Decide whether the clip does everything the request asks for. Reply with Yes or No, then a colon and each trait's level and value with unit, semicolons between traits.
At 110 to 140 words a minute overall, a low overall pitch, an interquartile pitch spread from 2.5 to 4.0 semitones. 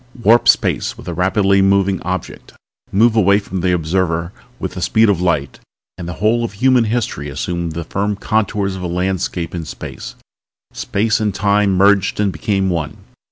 No: average, 175 wpm; very low, 95 Hz; average, 2.8 semitones